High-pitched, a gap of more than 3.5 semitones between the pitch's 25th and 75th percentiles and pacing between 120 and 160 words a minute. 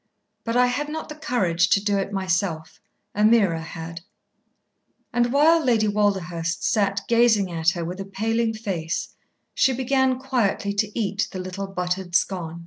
Yes: high, 200 Hz; average, 4.7 semitones; average, 155 wpm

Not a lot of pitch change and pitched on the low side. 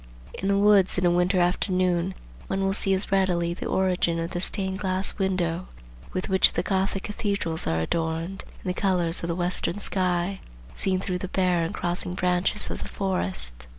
No: narrow, 1.9 semitones; medium, 185 Hz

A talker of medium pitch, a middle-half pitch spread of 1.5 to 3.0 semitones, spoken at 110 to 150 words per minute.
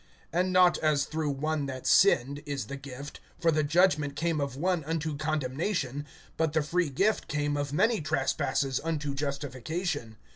No: medium, 150 Hz; average, 2.7 semitones; average, 160 wpm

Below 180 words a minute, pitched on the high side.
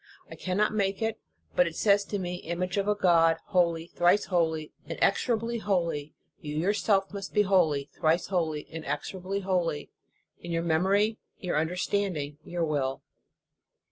No: average, 150 wpm; medium, 180 Hz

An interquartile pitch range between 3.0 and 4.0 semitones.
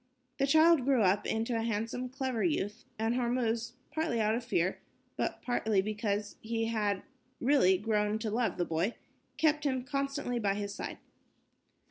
Yes: average, 3.4 semitones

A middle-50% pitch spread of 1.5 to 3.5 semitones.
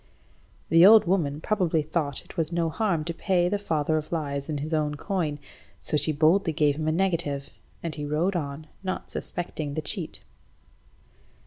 Yes: average, 2.9 semitones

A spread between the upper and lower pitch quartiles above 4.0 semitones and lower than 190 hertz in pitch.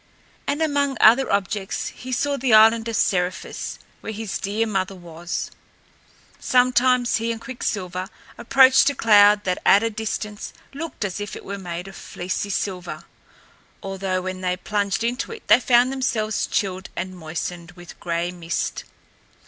No: average, 4.5 semitones; high, 205 Hz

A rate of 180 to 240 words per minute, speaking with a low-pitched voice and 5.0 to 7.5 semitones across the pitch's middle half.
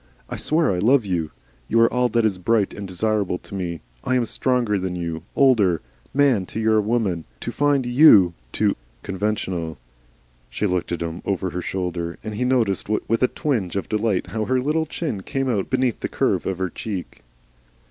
Yes: average, 190 wpm; low, 105 Hz; wide, 5.4 semitones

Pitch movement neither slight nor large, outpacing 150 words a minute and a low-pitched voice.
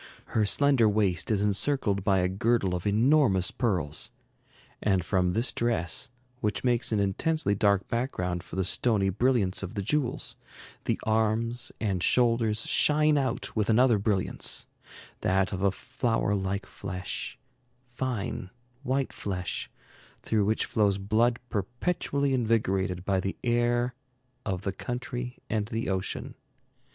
No: average, 4.0 semitones; slow, 135 wpm; low, 105 Hz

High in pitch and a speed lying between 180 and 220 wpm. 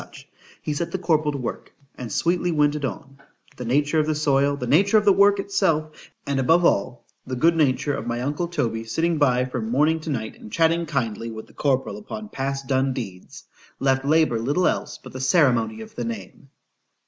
No: medium, 140 Hz; average, 185 wpm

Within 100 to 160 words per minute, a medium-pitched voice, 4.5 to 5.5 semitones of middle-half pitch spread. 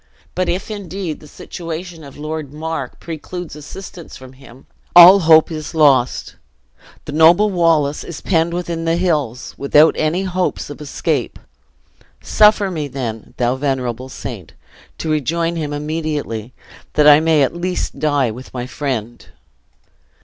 No: average, 140 wpm; medium, 155 Hz; average, 3.7 semitones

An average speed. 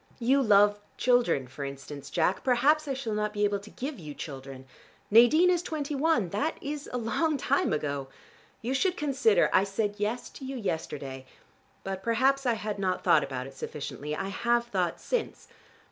Yes: average, 180 wpm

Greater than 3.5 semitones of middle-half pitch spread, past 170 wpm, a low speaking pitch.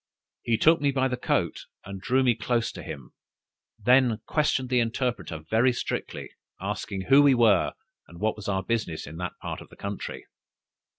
Yes: average, 4.6 semitones; average, 180 wpm; low, 115 Hz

